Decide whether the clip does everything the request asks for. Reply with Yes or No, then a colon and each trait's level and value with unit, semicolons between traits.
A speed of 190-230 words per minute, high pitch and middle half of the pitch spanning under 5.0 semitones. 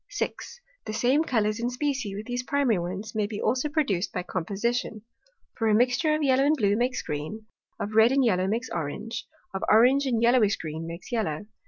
Yes: average, 195 wpm; high, 225 Hz; average, 4.3 semitones